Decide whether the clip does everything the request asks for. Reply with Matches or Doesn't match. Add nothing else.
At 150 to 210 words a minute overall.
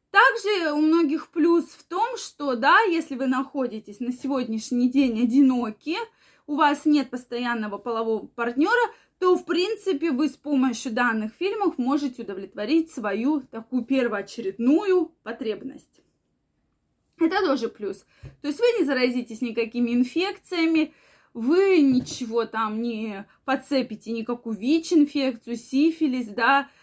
Doesn't match